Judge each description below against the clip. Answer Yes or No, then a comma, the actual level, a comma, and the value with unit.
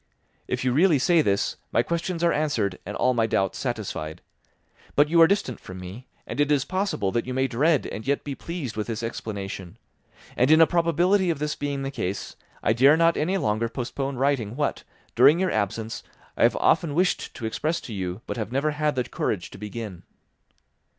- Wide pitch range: Yes, wide, 6.0 semitones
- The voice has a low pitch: Yes, low, 130 Hz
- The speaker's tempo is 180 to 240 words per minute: Yes, fast, 205 wpm